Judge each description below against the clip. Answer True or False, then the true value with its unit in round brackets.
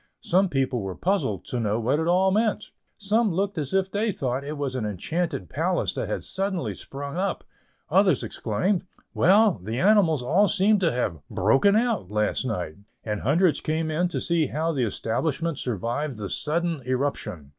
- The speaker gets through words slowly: False (175 wpm)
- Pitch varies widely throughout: True (7.6 semitones)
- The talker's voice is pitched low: False (155 Hz)